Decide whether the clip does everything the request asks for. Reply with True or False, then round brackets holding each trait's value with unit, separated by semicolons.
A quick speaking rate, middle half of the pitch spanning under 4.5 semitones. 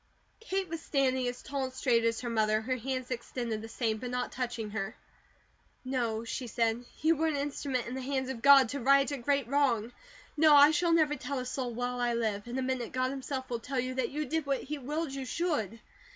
True (230 wpm; 2.9 semitones)